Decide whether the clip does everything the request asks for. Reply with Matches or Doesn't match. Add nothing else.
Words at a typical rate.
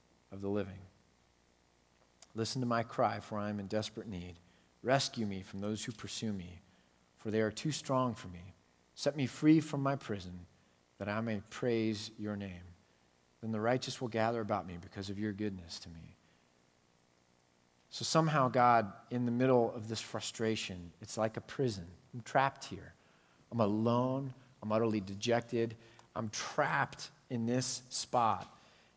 Matches